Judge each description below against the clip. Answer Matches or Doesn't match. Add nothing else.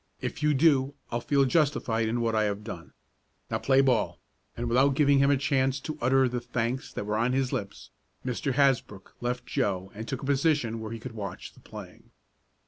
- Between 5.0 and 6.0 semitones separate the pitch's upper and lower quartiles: Doesn't match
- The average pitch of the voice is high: Doesn't match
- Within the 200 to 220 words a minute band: Matches